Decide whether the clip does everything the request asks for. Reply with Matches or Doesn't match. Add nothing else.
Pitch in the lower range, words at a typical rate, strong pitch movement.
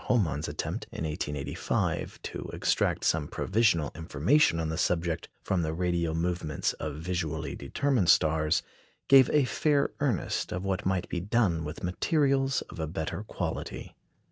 Matches